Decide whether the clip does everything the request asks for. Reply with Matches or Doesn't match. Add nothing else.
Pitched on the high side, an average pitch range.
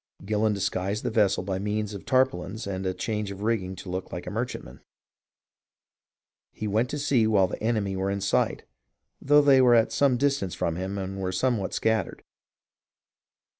Doesn't match